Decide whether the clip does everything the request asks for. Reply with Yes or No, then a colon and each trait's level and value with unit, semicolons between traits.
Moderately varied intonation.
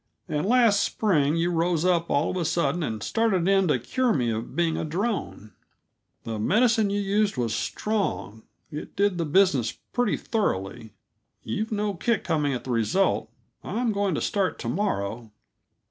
No: wide, 8.6 semitones